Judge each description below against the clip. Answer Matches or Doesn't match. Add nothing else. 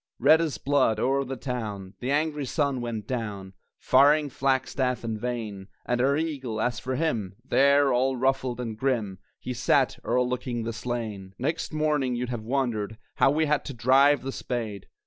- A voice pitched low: Matches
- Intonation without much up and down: Doesn't match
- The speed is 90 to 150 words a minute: Doesn't match